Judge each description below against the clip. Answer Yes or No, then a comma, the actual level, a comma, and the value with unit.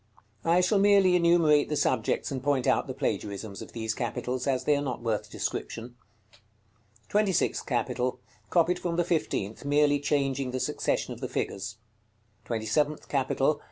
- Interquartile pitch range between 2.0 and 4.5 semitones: No, average, 5.3 semitones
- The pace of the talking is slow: No, average, 170 wpm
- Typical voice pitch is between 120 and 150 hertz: Yes, low, 135 Hz